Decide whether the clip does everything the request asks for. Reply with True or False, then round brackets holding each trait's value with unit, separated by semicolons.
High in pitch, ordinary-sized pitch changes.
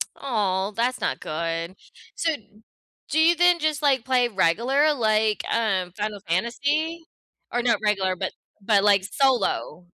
False (225 Hz; 6.2 semitones)